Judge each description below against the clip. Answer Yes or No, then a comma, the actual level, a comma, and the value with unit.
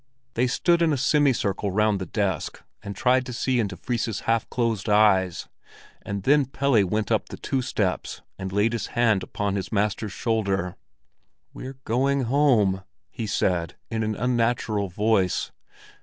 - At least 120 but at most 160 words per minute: Yes, average, 155 wpm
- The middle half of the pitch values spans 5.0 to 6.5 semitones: No, average, 4.0 semitones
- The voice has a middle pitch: No, low, 110 Hz